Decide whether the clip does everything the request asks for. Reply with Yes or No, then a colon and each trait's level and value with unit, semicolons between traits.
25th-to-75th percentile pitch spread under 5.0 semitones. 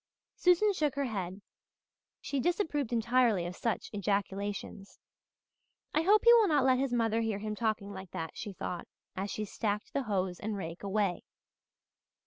No: wide, 5.5 semitones